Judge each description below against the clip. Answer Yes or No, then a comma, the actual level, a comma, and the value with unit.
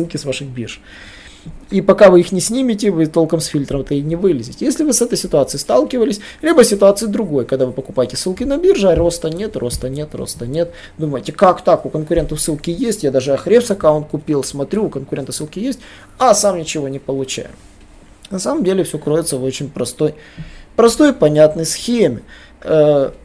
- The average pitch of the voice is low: No, medium, 160 Hz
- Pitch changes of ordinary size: No, wide, 6.3 semitones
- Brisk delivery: Yes, fast, 190 wpm